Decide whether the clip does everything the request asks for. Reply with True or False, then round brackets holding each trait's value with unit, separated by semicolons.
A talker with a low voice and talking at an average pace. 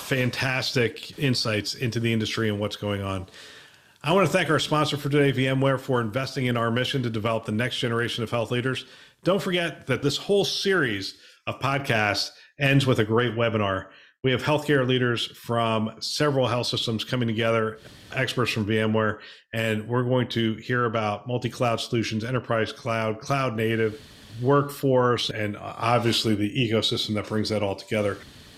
True (120 Hz; 170 wpm)